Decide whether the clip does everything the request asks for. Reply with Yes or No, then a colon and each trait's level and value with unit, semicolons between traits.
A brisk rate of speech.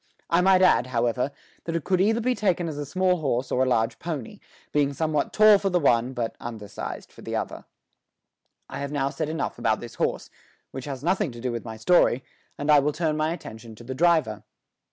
Yes: fast, 220 wpm